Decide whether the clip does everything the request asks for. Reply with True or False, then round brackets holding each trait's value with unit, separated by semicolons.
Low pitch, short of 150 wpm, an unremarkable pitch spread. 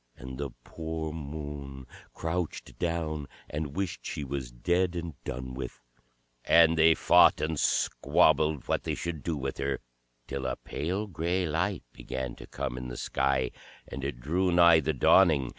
False (75 Hz; 160 wpm; 3.7 semitones)